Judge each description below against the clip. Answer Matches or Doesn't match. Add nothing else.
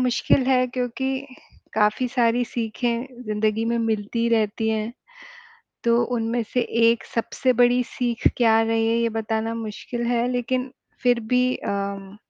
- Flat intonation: Matches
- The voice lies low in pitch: Doesn't match